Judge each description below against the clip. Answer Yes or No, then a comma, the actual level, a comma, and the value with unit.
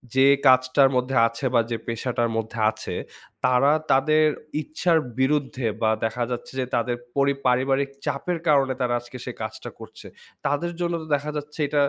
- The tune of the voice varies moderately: Yes, average, 3.0 semitones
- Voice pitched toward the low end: Yes, low, 130 Hz